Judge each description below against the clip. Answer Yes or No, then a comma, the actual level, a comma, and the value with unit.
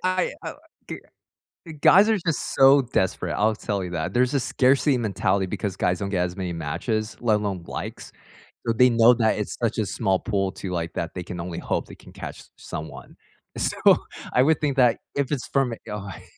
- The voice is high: No, low, 110 Hz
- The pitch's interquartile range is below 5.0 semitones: No, average, 5.3 semitones